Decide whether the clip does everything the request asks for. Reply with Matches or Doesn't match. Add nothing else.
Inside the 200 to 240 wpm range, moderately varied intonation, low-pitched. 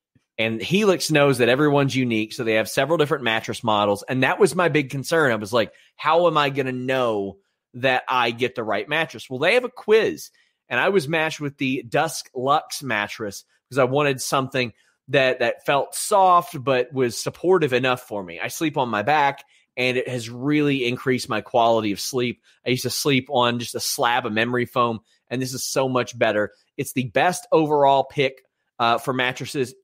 Matches